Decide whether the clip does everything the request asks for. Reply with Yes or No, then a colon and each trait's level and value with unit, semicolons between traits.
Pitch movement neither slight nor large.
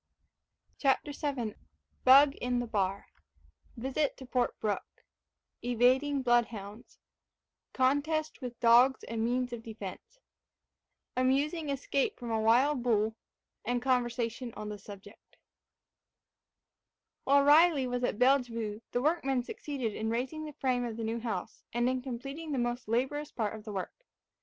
Yes: average, 3.2 semitones